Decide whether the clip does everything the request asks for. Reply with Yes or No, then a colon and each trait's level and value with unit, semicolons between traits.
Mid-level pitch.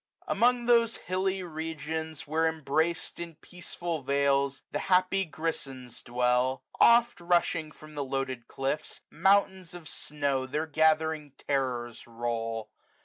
Yes: medium, 155 Hz